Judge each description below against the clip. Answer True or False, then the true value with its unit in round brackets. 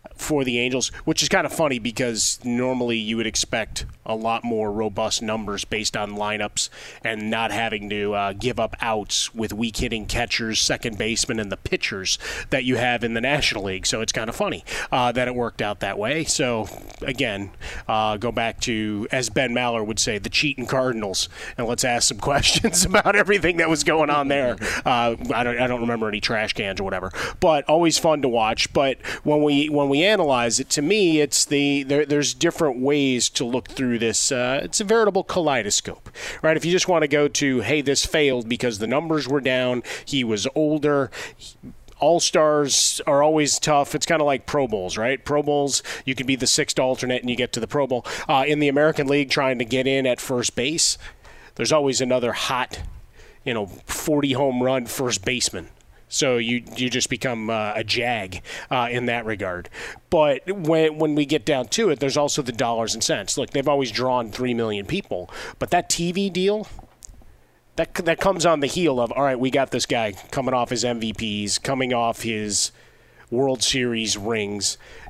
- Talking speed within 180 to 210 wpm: True (200 wpm)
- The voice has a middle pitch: False (125 Hz)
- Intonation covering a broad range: False (4.4 semitones)